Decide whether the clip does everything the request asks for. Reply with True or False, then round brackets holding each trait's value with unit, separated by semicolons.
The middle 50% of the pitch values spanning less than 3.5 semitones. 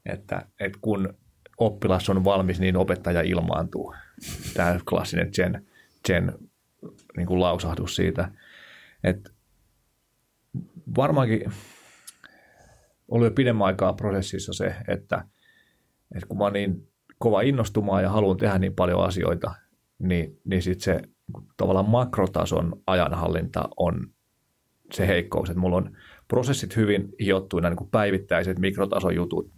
True (2.4 semitones)